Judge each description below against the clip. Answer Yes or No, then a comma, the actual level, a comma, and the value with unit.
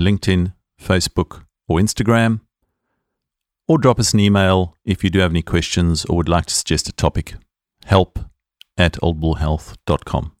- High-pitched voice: No, very low, 95 Hz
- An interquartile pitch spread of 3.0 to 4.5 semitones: Yes, average, 3.3 semitones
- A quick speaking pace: No, average, 145 wpm